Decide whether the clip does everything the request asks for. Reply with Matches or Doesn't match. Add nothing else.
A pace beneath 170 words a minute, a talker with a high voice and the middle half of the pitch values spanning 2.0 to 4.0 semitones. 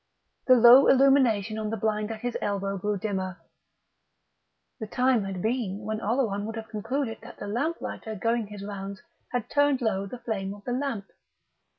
Doesn't match